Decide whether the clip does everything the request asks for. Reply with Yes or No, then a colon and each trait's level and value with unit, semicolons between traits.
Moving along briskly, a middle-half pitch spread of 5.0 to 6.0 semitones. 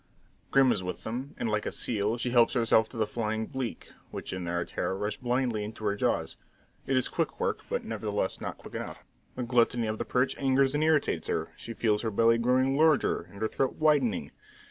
No: fast, 210 wpm; average, 3.4 semitones